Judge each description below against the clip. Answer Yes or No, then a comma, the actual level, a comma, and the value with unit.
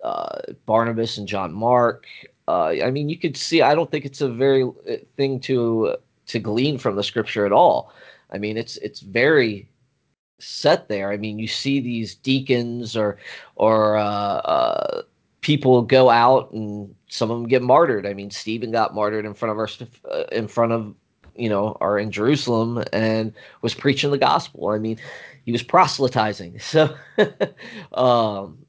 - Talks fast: No, average, 170 wpm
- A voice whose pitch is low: Yes, low, 115 Hz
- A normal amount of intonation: Yes, average, 3.9 semitones